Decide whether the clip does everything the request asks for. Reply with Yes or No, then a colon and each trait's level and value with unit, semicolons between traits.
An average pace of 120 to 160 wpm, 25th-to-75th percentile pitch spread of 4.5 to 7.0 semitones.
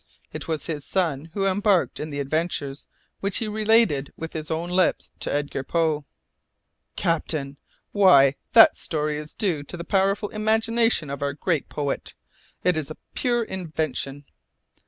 Yes: average, 155 wpm; average, 5.2 semitones